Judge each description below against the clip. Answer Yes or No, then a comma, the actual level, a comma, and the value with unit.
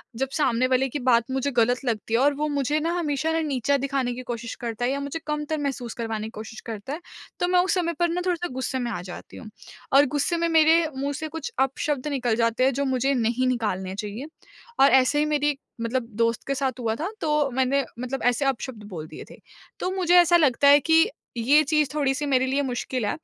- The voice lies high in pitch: Yes, very high, 270 Hz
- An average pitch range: Yes, average, 3.6 semitones